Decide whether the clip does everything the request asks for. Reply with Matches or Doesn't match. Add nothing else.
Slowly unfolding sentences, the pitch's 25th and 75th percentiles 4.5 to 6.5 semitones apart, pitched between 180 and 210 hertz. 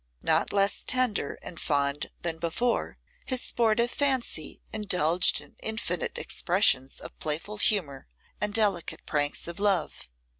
Matches